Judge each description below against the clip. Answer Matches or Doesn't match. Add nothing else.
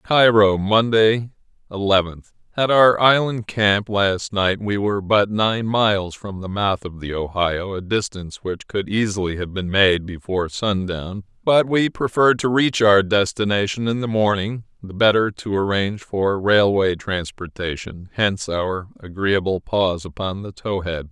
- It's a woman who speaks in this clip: Doesn't match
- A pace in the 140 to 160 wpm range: Matches